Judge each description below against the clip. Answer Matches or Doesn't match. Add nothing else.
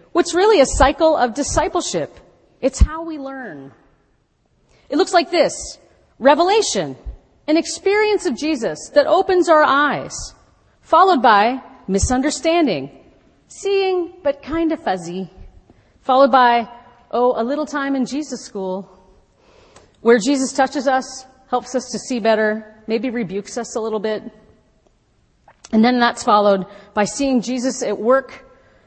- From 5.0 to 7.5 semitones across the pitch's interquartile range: Matches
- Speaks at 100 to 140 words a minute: Matches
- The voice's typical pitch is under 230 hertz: Doesn't match